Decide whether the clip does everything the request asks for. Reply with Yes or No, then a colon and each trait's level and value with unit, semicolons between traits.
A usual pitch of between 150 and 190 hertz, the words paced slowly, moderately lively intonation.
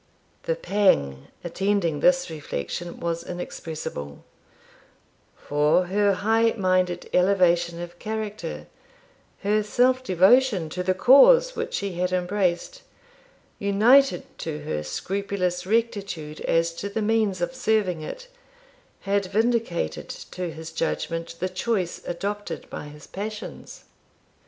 Yes: medium, 185 Hz; slow, 115 wpm; average, 4.1 semitones